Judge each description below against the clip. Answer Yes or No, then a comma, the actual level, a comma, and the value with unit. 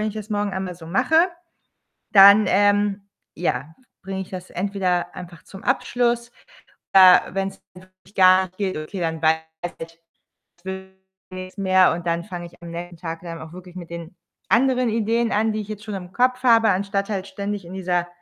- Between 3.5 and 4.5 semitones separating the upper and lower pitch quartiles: No, average, 2.8 semitones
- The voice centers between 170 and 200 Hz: Yes, high, 190 Hz